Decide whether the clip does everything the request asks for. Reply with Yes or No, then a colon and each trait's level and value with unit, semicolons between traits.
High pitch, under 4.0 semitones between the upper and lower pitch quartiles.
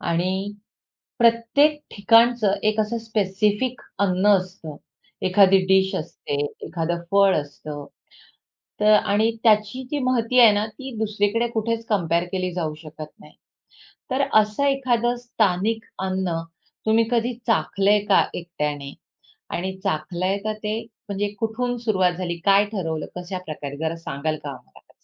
No: high, 200 Hz; average, 4.3 semitones